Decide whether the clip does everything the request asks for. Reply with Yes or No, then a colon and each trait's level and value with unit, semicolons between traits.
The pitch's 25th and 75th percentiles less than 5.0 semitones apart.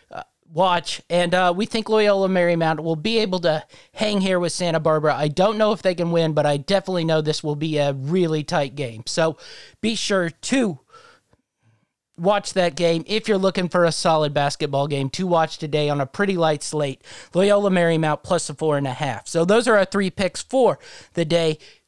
Yes: average, 3.9 semitones